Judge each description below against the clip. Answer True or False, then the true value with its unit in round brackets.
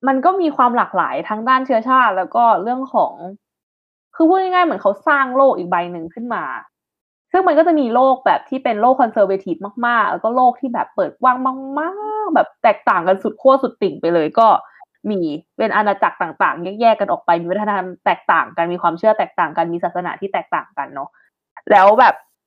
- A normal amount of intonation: False (6.5 semitones)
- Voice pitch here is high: True (235 Hz)